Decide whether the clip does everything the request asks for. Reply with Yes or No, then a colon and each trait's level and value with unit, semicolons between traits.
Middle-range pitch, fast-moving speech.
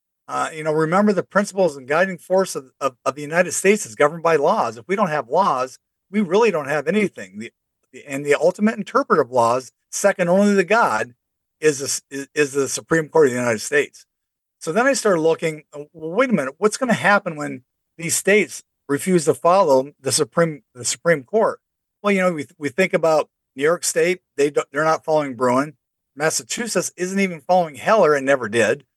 Yes: medium, 160 Hz; fast, 210 wpm